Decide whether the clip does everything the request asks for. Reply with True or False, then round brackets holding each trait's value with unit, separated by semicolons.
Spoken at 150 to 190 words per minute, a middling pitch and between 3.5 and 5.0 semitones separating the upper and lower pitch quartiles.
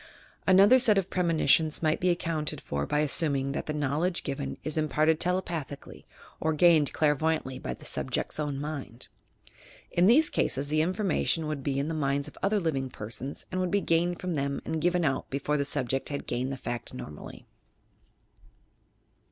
True (175 wpm; 155 Hz; 3.8 semitones)